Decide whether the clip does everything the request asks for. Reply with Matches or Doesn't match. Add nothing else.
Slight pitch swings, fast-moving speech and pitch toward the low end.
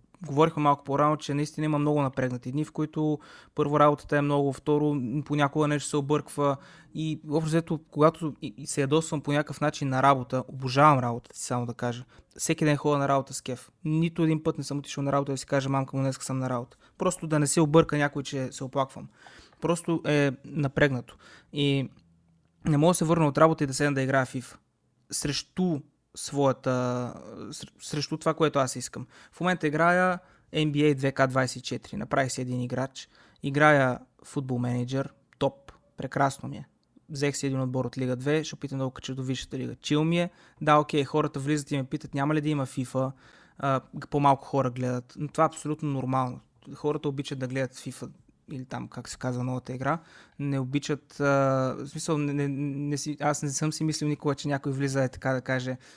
Doesn't match